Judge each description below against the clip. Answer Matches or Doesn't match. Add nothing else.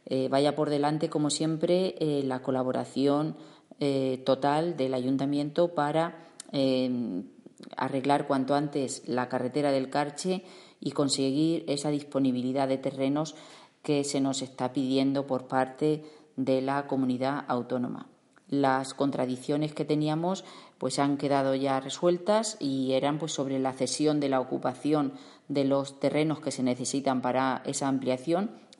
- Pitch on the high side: Doesn't match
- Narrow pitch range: Matches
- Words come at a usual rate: Matches